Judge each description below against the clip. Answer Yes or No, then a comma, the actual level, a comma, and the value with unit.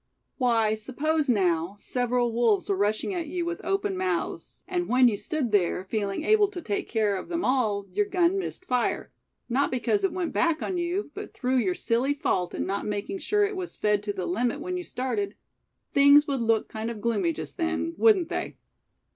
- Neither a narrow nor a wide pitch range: No, wide, 8.4 semitones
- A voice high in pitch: Yes, very high, 260 Hz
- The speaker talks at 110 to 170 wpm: No, average, 200 wpm